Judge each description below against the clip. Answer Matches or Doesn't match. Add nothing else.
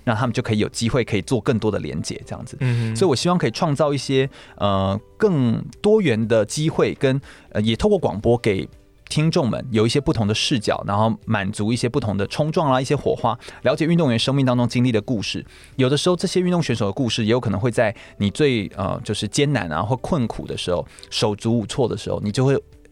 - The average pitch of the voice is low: Matches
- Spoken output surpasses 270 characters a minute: Matches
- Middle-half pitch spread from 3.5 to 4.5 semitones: Doesn't match